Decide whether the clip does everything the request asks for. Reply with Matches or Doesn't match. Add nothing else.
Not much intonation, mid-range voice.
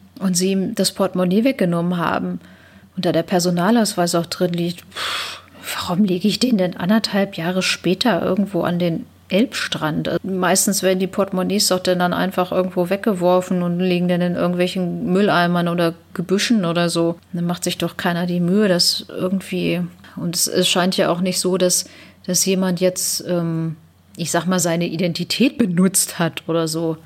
Matches